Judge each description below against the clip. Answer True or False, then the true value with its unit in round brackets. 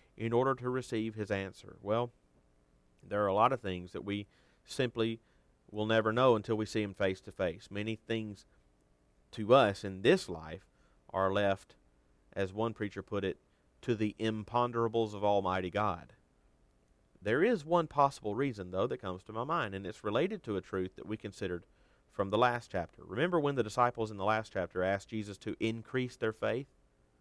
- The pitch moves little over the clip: False (4.1 semitones)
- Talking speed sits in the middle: True (185 wpm)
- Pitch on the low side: True (105 Hz)